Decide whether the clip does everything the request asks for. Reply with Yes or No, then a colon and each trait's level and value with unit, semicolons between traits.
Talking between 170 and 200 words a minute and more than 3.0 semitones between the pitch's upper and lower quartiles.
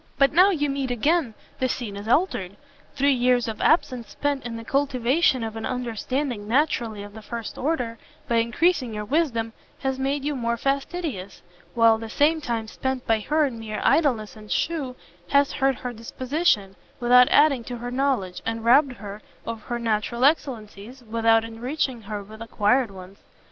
Yes: average, 175 wpm; average, 3.7 semitones